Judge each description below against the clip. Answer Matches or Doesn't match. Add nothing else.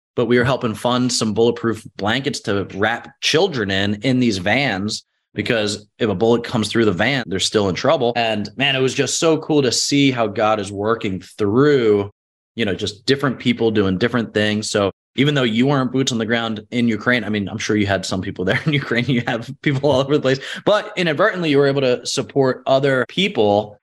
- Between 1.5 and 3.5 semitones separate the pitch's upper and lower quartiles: Doesn't match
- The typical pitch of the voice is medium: Doesn't match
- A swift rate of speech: Matches